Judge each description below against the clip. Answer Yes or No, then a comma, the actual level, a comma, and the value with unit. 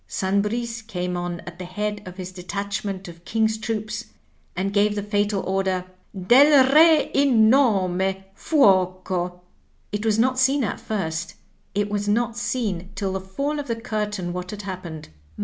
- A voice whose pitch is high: Yes, high, 205 Hz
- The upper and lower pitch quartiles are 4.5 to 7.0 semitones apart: No, average, 3.5 semitones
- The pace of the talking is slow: No, average, 165 wpm